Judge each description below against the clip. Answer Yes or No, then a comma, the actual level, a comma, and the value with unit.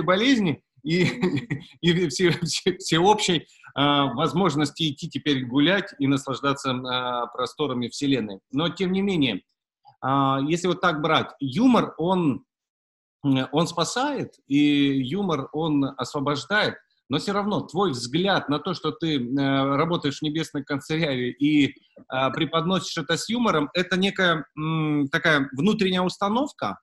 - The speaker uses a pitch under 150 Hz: No, medium, 155 Hz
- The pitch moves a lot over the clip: No, average, 4.5 semitones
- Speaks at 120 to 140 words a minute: Yes, average, 130 wpm